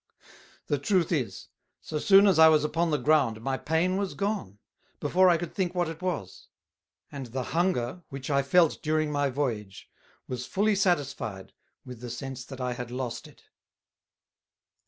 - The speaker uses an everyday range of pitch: No, wide, 5.7 semitones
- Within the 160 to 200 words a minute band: Yes, average, 170 wpm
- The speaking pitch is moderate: Yes, medium, 145 Hz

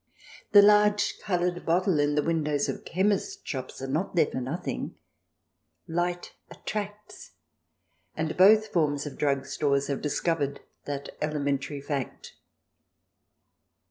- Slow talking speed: Yes, slow, 120 wpm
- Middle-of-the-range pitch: Yes, medium, 155 Hz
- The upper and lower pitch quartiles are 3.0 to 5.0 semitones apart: Yes, average, 4.7 semitones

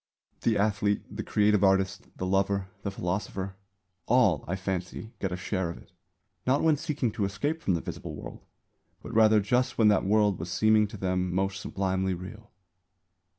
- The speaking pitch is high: No, low, 100 Hz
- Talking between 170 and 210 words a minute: Yes, average, 175 wpm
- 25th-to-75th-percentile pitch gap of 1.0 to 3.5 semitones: Yes, narrow, 2.4 semitones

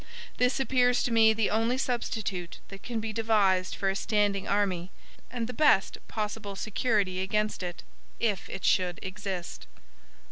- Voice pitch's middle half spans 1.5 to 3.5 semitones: Yes, average, 2.9 semitones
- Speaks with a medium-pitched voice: No, high, 210 Hz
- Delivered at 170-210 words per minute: No, average, 150 wpm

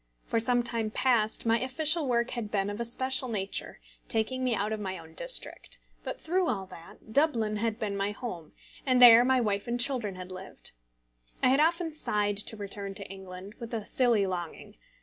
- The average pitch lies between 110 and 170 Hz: No, high, 225 Hz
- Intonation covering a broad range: No, average, 4.0 semitones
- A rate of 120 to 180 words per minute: No, average, 195 wpm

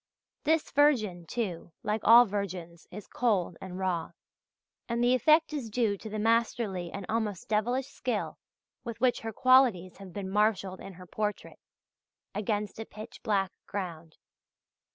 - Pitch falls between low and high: No, high, 210 Hz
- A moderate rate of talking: Yes, average, 150 wpm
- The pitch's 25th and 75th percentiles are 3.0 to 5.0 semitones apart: Yes, average, 3.9 semitones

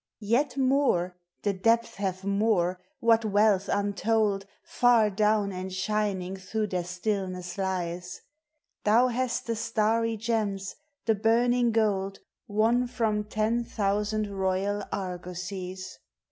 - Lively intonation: No, average, 3.0 semitones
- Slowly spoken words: Yes, slow, 115 wpm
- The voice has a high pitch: Yes, high, 210 Hz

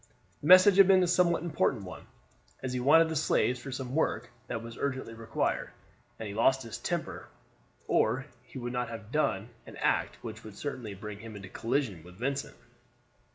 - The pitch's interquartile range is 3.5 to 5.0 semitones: Yes, average, 4.7 semitones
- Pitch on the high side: No, low, 125 Hz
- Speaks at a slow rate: No, average, 190 wpm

